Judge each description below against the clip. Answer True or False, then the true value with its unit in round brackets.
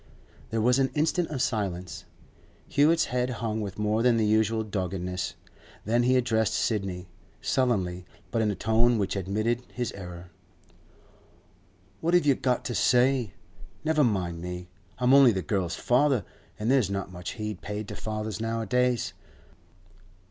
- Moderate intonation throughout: True (4.4 semitones)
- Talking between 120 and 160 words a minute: True (150 wpm)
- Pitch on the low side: True (110 Hz)